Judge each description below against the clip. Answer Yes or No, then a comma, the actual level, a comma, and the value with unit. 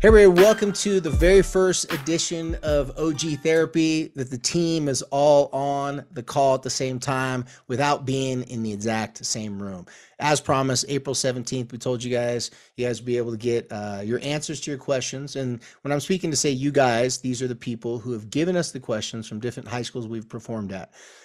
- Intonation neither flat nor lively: Yes, average, 3.6 semitones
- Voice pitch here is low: Yes, low, 130 Hz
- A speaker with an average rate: No, fast, 215 wpm